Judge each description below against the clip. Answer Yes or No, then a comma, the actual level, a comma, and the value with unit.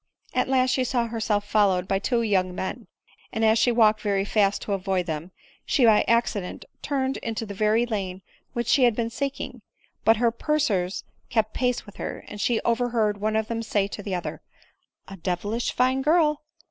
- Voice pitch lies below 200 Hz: No, high, 220 Hz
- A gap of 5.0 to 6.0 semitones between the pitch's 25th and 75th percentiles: No, average, 3.2 semitones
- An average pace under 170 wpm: No, fast, 205 wpm